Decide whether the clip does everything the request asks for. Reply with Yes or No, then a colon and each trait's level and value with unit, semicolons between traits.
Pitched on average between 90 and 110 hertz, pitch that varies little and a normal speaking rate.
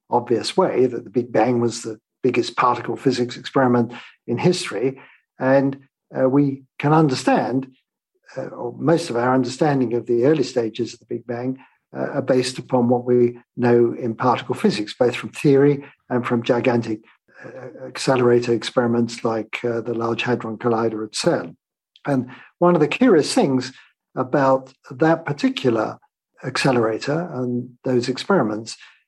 No: low, 125 Hz; narrow, 2.1 semitones; average, 150 wpm